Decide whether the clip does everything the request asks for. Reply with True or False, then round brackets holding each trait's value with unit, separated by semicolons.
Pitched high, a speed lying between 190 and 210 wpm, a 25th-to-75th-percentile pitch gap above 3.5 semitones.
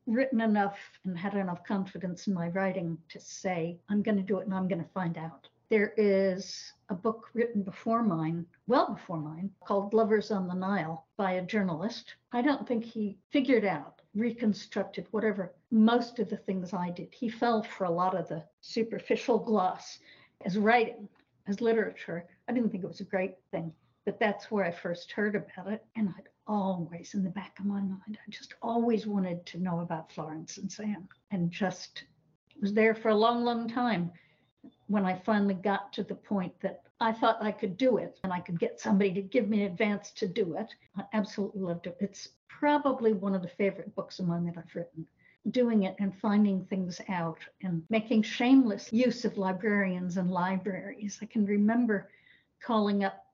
False (200 Hz; 195 wpm; 3.1 semitones)